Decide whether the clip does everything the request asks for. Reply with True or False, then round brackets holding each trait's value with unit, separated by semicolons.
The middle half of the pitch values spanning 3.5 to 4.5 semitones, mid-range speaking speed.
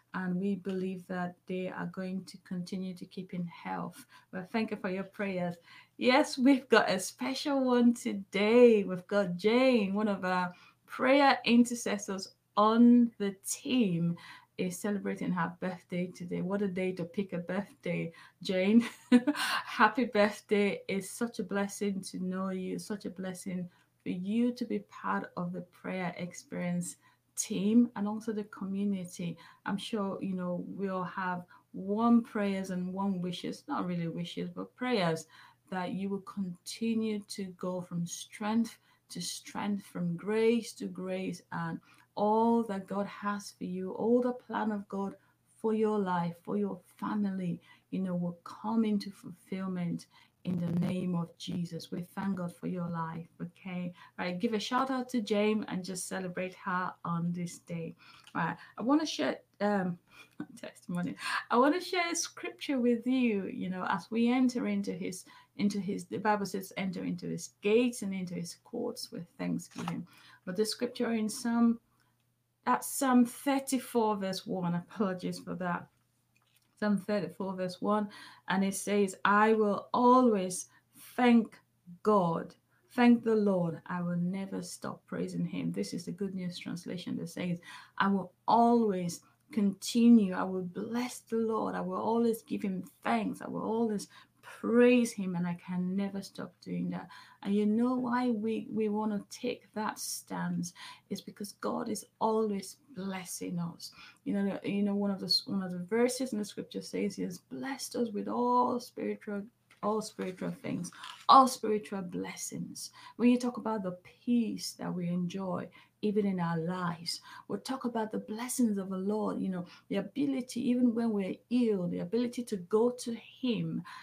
True (4.1 semitones; 170 wpm)